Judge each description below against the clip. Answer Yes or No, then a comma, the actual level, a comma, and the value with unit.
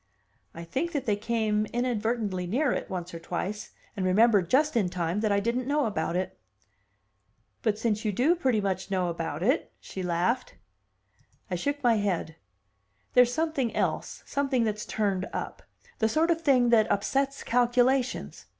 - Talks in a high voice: Yes, high, 220 Hz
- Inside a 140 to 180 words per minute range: Yes, average, 165 wpm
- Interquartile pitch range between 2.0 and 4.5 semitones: No, average, 5.2 semitones